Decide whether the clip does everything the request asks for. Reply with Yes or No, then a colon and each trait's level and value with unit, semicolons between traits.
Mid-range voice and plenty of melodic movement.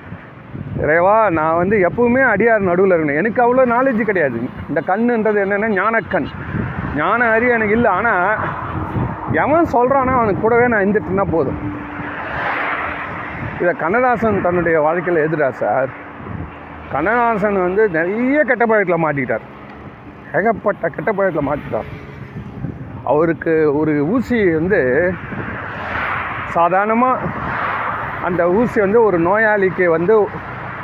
No: high, 195 Hz; wide, 6.4 semitones